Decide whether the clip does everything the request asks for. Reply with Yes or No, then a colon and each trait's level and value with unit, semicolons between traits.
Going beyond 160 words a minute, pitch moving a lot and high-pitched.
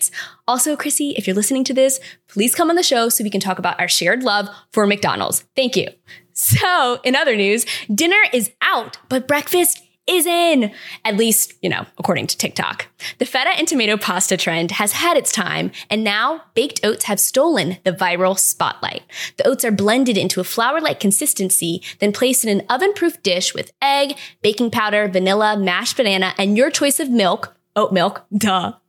Yes: average, 185 wpm; wide, 5.8 semitones; high, 220 Hz